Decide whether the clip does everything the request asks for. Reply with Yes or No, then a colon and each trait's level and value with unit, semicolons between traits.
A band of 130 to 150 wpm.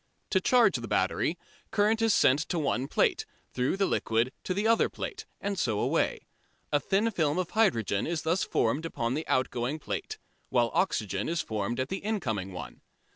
No: average, 180 wpm